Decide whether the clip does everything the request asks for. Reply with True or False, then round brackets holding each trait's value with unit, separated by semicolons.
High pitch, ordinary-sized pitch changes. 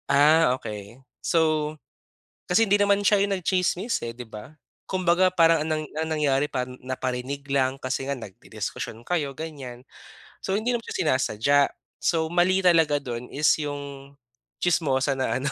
False (150 Hz; 4.9 semitones)